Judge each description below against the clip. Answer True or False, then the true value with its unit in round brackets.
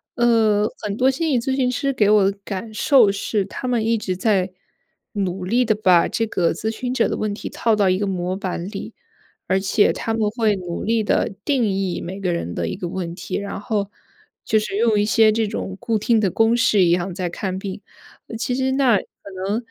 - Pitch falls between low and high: False (210 Hz)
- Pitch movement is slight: False (3.2 semitones)